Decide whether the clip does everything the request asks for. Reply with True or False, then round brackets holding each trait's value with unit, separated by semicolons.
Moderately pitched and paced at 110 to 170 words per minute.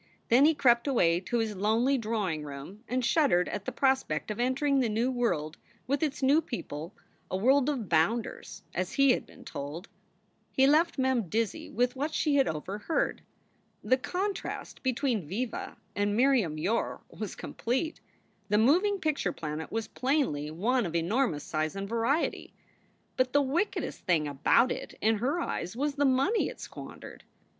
False (235 Hz; 165 wpm)